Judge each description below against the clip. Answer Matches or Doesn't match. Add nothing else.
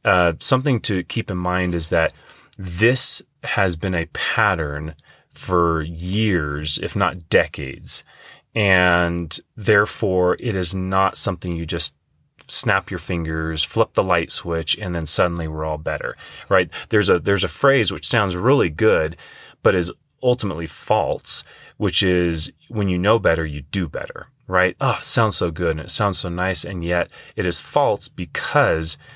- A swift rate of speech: Doesn't match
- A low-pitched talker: Matches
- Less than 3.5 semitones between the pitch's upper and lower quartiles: Matches